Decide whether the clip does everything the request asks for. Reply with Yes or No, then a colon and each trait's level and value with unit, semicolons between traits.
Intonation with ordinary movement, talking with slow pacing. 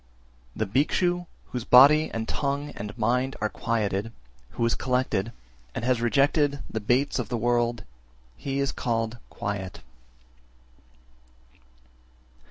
Yes: average, 3.5 semitones; slow, 125 wpm